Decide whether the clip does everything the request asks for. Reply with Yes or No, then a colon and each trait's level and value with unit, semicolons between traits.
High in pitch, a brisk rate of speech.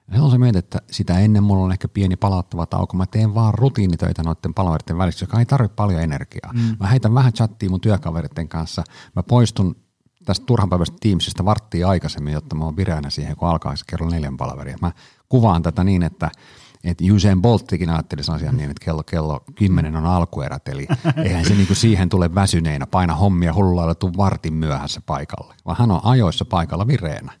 No: very low, 95 Hz; fast, 195 wpm